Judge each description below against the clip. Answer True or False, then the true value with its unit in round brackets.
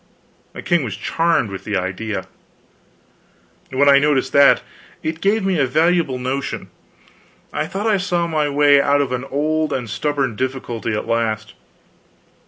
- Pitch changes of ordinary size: True (4.6 semitones)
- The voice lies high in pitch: False (140 Hz)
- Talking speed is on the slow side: False (155 wpm)